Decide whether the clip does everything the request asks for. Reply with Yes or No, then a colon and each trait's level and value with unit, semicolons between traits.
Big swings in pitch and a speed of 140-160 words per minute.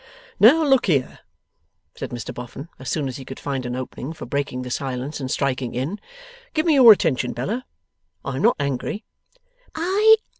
No: wide, 8.2 semitones; average, 175 wpm